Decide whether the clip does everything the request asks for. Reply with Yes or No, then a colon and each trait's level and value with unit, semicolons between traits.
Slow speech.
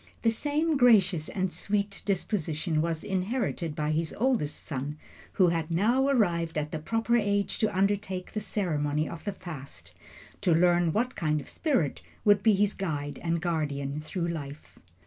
No: average, 165 wpm